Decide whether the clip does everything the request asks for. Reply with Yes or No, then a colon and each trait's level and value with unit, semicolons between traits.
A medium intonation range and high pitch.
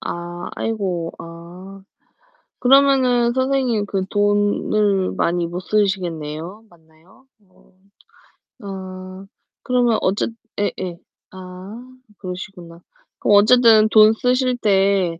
Yes: average, 3.8 semitones; high, 195 Hz